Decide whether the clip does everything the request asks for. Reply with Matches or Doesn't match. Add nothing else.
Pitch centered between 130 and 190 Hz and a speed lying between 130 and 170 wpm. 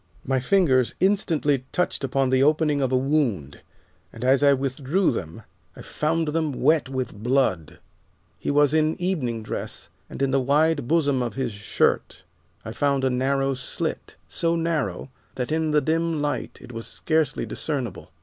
Matches